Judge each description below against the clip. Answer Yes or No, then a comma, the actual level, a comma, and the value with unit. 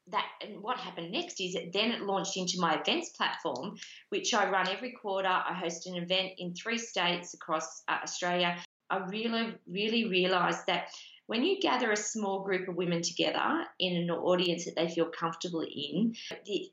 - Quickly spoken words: No, average, 185 wpm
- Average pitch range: Yes, average, 3.7 semitones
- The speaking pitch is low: No, medium, 185 Hz